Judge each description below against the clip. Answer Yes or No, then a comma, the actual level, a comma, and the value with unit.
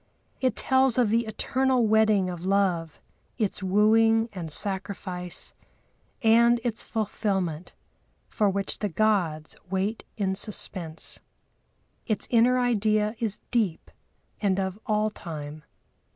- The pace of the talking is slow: Yes, slow, 115 wpm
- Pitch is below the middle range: No, high, 210 Hz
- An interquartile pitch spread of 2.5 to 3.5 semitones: Yes, average, 3.1 semitones